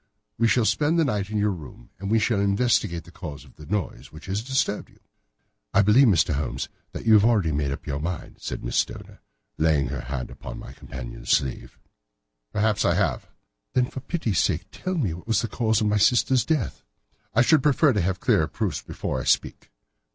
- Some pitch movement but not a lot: No, wide, 7.0 semitones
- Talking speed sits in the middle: No, fast, 210 wpm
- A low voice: Yes, low, 100 Hz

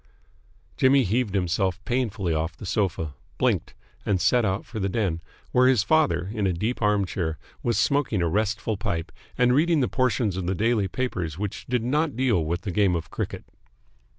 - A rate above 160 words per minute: Yes, average, 185 wpm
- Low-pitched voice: Yes, low, 105 Hz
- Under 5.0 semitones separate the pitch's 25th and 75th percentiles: No, average, 5.3 semitones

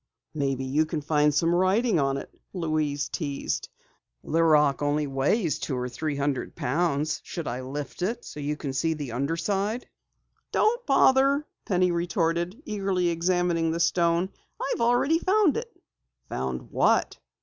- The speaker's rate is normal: Yes, average, 160 wpm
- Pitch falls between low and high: Yes, medium, 165 Hz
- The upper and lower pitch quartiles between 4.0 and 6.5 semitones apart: Yes, average, 4.7 semitones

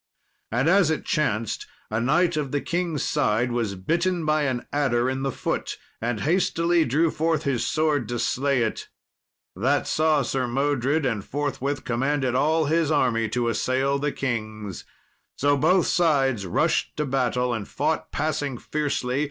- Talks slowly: No, average, 160 wpm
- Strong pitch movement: No, average, 4.1 semitones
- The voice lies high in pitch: No, medium, 140 Hz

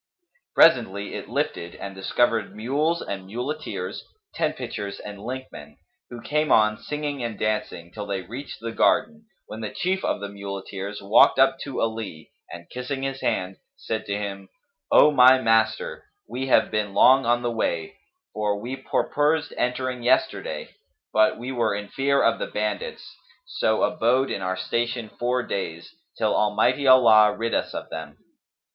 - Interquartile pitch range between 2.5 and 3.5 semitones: No, average, 4.7 semitones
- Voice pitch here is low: Yes, low, 115 Hz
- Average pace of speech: Yes, average, 160 wpm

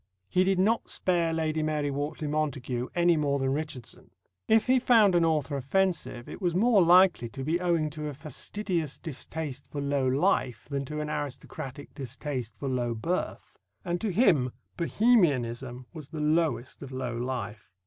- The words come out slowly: No, average, 170 wpm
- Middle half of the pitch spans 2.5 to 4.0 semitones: No, average, 4.7 semitones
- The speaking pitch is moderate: Yes, medium, 150 Hz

